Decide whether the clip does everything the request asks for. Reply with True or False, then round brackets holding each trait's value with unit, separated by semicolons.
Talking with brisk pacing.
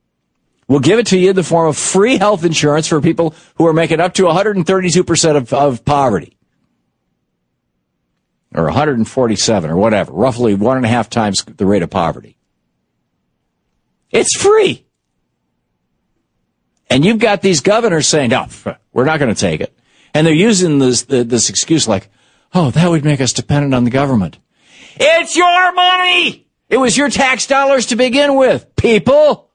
False (160 wpm)